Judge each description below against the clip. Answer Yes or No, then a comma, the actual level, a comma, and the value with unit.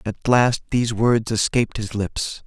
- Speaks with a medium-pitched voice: No, low, 115 Hz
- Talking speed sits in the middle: Yes, average, 170 wpm